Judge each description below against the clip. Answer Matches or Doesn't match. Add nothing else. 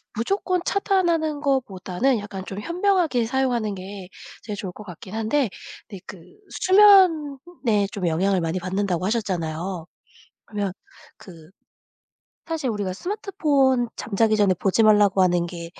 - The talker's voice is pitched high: Matches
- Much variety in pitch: Matches